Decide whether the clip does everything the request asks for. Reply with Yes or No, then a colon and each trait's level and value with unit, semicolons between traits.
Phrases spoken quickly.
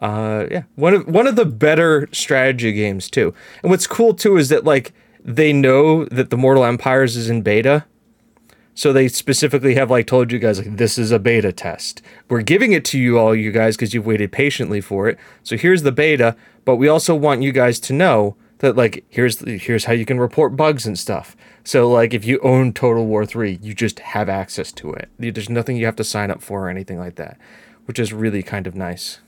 Yes: fast, 225 wpm